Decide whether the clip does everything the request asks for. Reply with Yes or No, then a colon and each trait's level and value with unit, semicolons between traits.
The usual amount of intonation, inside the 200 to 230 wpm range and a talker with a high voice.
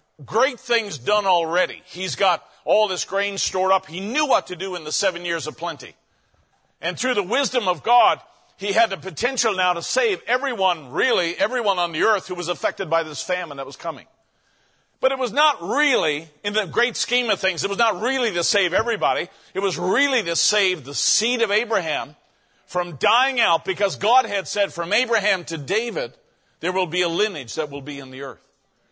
Yes: average, 4.8 semitones; fast, 205 wpm; high, 195 Hz